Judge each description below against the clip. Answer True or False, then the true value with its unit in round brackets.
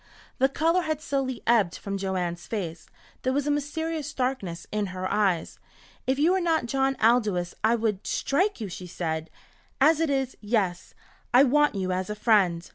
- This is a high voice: True (230 Hz)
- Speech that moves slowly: False (180 wpm)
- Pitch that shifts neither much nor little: False (7.2 semitones)